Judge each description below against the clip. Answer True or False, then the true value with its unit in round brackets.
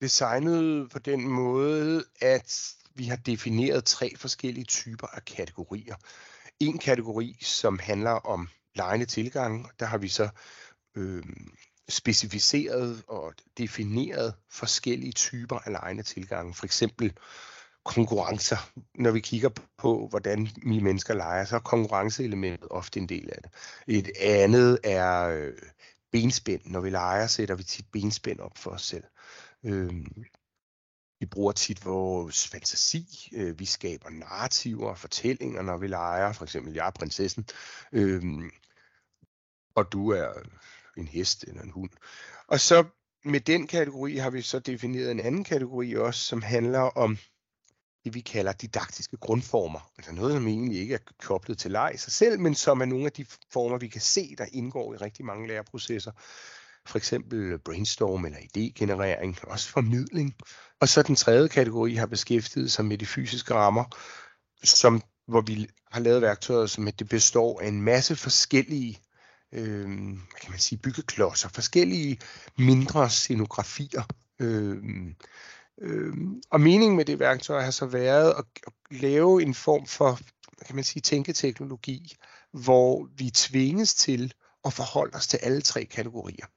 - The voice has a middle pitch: False (115 Hz)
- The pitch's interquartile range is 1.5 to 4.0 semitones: False (4.4 semitones)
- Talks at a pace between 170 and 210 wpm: False (150 wpm)